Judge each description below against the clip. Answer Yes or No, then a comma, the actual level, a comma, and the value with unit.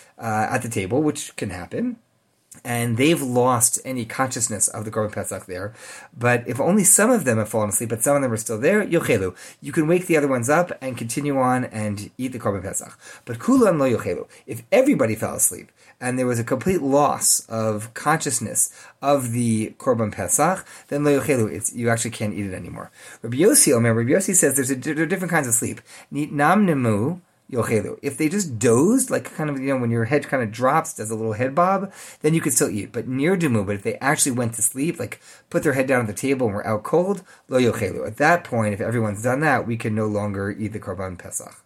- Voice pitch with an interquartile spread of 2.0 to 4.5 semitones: No, average, 5.2 semitones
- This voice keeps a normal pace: No, fast, 230 wpm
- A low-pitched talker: Yes, low, 125 Hz